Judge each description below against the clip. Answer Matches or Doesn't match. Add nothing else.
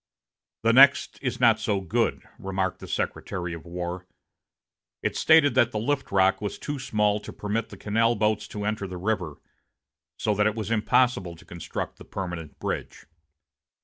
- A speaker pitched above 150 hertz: Doesn't match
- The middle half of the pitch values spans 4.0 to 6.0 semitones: Doesn't match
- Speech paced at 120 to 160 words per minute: Doesn't match